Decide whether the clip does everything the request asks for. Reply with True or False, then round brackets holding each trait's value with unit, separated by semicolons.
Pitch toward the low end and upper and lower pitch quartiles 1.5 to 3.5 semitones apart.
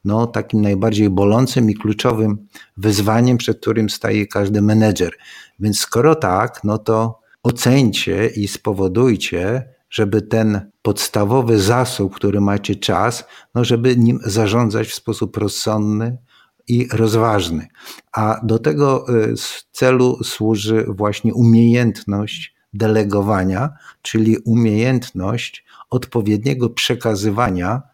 True (110 Hz; 2.6 semitones)